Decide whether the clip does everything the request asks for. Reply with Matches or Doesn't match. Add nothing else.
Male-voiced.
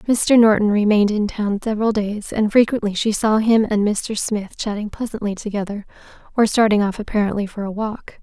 Doesn't match